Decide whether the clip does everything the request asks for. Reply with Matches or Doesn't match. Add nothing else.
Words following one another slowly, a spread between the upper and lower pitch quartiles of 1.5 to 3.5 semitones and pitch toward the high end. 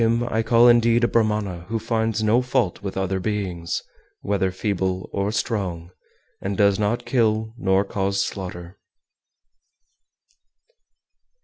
Doesn't match